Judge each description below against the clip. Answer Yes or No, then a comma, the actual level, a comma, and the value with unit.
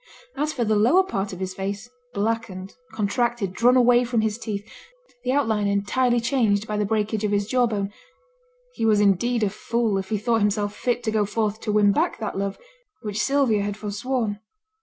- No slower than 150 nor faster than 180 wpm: No, average, 195 wpm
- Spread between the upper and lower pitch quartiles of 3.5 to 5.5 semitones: No, average, 2.8 semitones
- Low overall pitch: No, high, 215 Hz